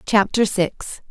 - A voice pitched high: Yes, high, 205 Hz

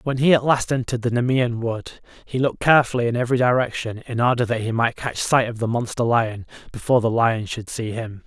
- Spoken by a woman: No, male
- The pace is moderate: No, fast, 225 wpm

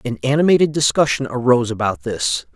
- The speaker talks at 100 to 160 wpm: Yes, average, 140 wpm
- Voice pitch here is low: Yes, low, 130 Hz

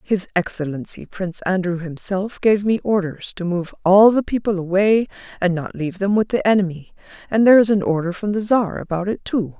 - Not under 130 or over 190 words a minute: No, average, 200 wpm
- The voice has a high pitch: Yes, high, 195 Hz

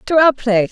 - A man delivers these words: No, female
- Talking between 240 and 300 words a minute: Yes, fast, 250 wpm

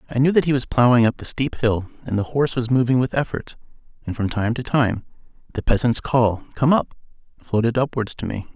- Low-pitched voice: Yes, low, 125 Hz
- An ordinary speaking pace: No, fast, 215 wpm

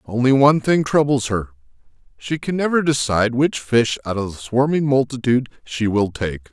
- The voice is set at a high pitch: No, low, 125 Hz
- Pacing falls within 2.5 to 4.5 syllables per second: No, 5.4 syllables/s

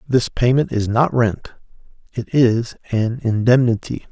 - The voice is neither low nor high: No, low, 120 Hz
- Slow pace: Yes, slow, 130 wpm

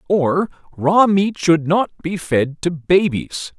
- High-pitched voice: No, medium, 170 Hz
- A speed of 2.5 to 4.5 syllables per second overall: Yes, 3.3 syllables/s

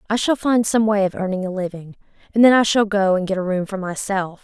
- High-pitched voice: Yes, high, 200 Hz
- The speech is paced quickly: Yes, fast, 270 wpm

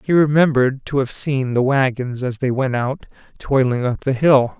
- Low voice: Yes, low, 130 Hz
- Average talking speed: Yes, average, 195 wpm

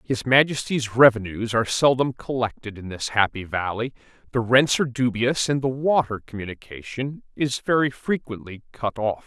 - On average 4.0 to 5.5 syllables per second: Yes, 5.0 syllables/s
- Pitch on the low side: Yes, low, 120 Hz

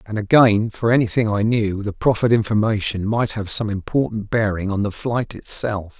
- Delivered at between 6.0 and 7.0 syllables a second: No, 5.1 syllables/s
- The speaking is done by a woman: No, male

